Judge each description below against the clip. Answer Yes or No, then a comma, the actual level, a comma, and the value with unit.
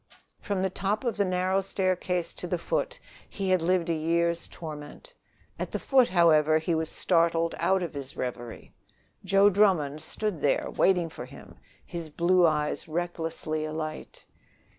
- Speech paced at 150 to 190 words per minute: Yes, average, 160 wpm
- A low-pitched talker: No, medium, 170 Hz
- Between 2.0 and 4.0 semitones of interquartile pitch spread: Yes, average, 3.2 semitones